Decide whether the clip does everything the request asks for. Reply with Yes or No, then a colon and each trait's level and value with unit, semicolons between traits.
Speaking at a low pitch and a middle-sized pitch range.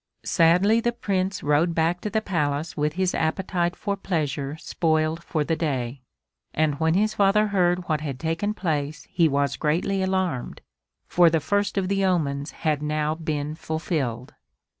No: medium, 165 Hz; average, 3.9 semitones